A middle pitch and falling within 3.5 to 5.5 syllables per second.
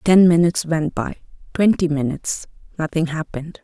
Yes: medium, 165 Hz; 5.4 syllables/s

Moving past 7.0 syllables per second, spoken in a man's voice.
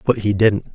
No: 4.8 syllables/s; male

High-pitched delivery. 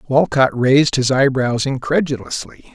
No: low, 130 Hz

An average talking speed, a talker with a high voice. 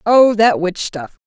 Yes: average, 190 wpm; high, 200 Hz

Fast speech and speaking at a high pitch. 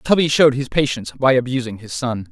No: fast, 210 wpm; low, 130 Hz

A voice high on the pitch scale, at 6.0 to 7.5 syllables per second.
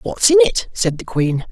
No: high, 215 Hz; 4.2 syllables/s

